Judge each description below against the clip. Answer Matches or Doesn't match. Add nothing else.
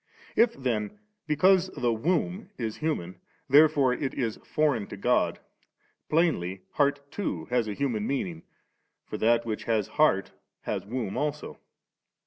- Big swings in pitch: Matches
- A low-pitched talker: Matches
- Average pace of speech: Matches